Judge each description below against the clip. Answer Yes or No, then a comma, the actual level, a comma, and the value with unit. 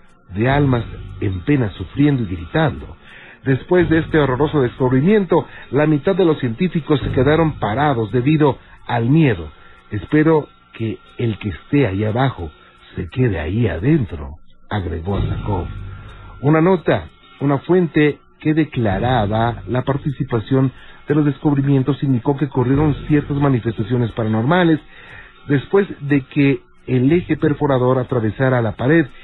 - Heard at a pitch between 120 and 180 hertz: Yes, low, 135 Hz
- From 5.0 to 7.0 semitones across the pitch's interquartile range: Yes, wide, 5.5 semitones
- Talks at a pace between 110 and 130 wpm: Yes, slow, 125 wpm